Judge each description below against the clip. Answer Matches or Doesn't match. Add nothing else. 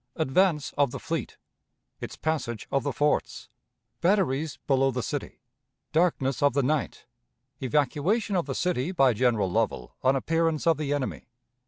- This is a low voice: Doesn't match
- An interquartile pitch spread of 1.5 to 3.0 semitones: Doesn't match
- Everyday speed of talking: Matches